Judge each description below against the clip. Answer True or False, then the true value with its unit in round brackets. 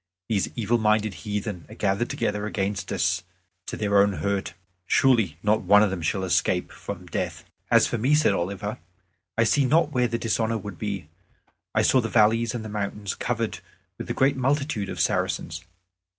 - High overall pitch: False (105 Hz)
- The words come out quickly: False (180 wpm)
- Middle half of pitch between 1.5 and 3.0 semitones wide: True (2.7 semitones)